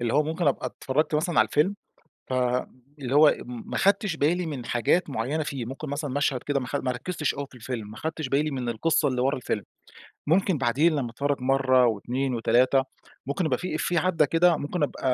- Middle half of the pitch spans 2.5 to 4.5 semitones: Yes, average, 3.7 semitones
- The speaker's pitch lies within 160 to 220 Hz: No, medium, 140 Hz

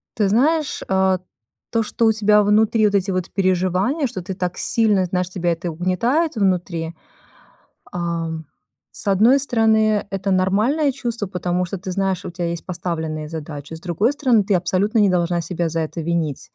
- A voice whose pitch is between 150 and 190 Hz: Yes, medium, 185 Hz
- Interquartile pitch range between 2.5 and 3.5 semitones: No, average, 3.9 semitones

